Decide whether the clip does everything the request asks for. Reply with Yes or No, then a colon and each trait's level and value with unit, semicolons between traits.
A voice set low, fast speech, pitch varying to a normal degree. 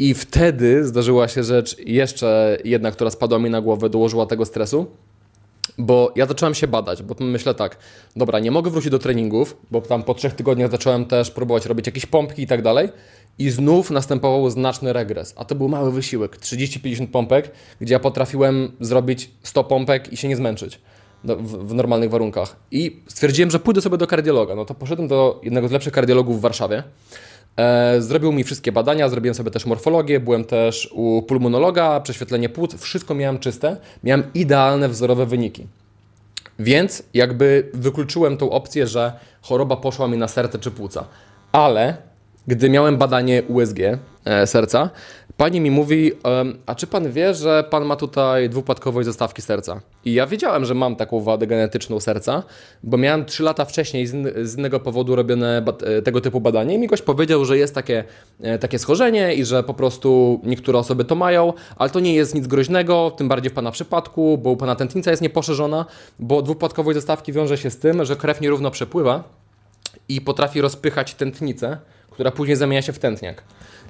Yes: low, 130 Hz; fast, 175 wpm; average, 3.7 semitones